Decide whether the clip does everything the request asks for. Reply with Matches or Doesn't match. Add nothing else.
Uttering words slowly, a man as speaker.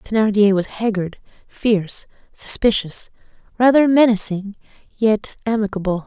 Doesn't match